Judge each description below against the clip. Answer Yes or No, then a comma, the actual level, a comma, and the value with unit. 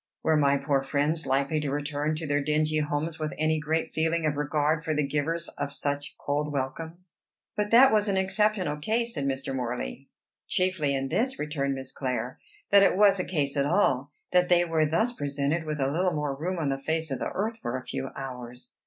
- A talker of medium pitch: Yes, medium, 150 Hz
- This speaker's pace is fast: Yes, fast, 210 wpm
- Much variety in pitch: No, average, 3.3 semitones